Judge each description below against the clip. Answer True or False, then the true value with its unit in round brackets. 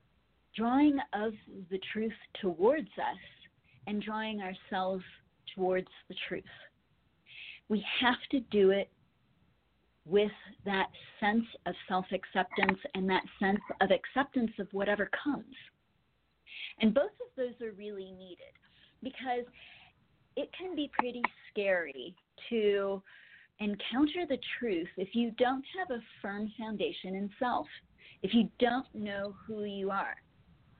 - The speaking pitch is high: True (210 Hz)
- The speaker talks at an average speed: False (125 wpm)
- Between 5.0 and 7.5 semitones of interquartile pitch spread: False (4.2 semitones)